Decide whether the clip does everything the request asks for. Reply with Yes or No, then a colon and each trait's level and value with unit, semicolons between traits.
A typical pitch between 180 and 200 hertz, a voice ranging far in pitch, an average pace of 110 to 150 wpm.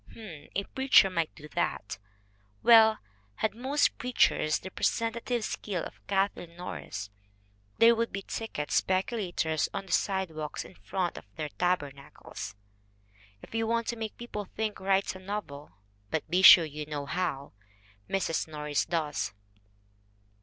Yes: medium, 185 Hz; wide, 6.1 semitones; average, 145 wpm